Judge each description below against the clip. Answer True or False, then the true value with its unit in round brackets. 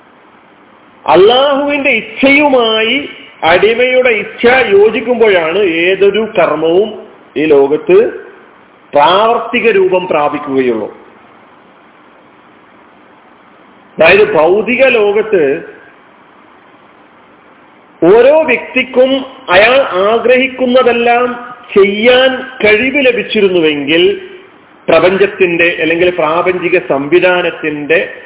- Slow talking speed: True (55 wpm)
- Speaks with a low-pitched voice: False (245 Hz)